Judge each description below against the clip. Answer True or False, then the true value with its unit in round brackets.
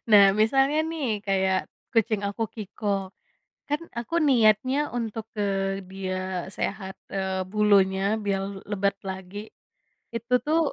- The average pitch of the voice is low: False (205 Hz)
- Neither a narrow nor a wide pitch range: True (3.2 semitones)